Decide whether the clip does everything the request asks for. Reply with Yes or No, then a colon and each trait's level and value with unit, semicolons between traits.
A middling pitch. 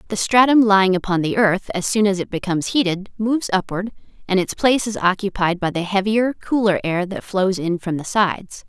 No: high, 195 Hz